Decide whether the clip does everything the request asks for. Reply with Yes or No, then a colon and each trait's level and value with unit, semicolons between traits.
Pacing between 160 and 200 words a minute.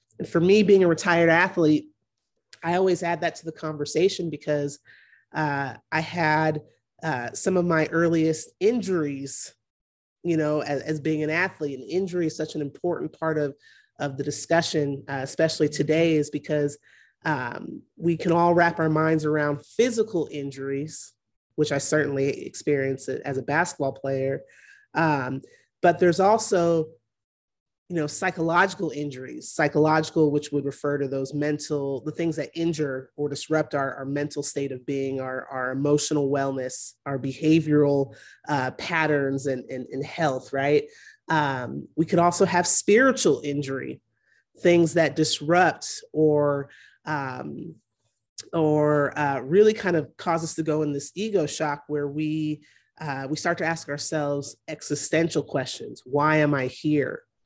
No: average, 150 wpm